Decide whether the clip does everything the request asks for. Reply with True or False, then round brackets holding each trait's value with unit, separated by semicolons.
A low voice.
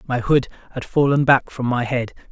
True (130 Hz)